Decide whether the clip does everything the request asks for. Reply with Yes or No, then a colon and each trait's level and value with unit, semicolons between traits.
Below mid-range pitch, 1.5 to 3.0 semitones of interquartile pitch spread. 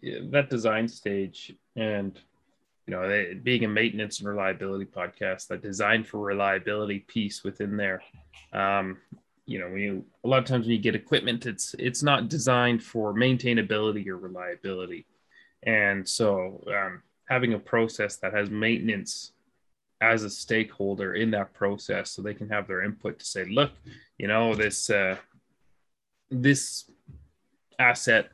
Yes: low, 105 Hz; average, 2.7 semitones